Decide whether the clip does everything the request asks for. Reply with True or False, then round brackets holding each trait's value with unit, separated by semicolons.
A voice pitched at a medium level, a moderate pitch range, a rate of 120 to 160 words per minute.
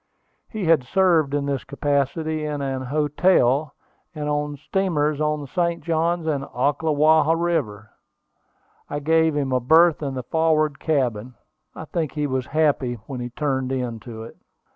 True (150 Hz; 3.1 semitones; 155 wpm)